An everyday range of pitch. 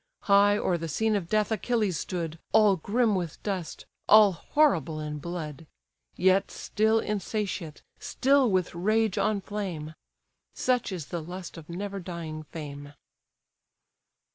Yes: average, 4.4 semitones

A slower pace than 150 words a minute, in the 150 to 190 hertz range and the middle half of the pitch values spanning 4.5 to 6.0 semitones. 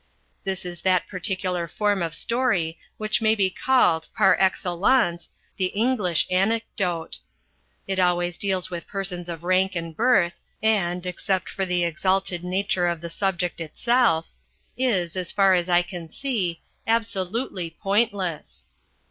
No: average, 140 wpm; medium, 185 Hz; average, 2.7 semitones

